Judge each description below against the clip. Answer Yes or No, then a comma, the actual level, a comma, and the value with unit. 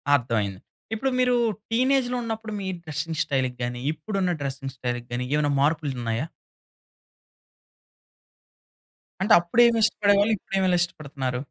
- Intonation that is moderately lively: No, wide, 8.7 semitones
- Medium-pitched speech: Yes, medium, 155 Hz